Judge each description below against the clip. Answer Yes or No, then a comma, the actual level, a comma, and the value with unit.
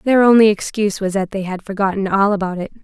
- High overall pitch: Yes, high, 200 Hz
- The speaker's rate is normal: No, fast, 235 wpm